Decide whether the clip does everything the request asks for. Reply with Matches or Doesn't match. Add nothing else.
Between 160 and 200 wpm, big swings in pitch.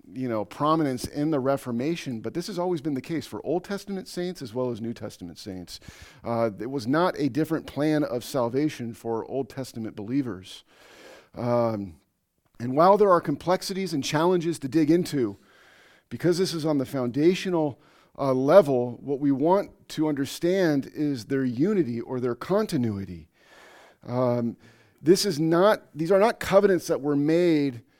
Matches